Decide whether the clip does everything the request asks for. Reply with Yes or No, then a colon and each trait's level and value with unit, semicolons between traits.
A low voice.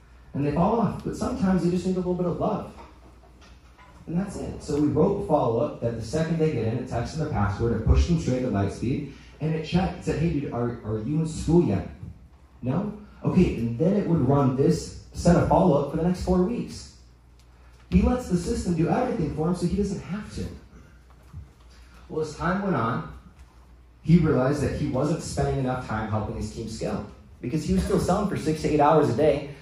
No: medium, 145 Hz